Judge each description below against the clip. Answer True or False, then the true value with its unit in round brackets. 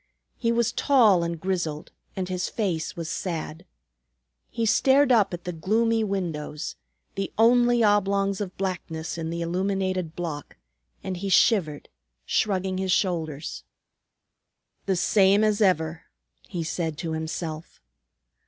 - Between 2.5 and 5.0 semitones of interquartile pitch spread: True (3.9 semitones)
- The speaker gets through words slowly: True (130 wpm)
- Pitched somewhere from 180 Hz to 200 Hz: True (185 Hz)